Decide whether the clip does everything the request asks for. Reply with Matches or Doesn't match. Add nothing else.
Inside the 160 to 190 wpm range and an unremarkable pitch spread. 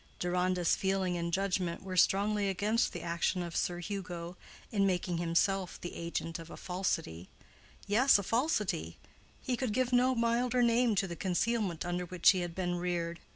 Matches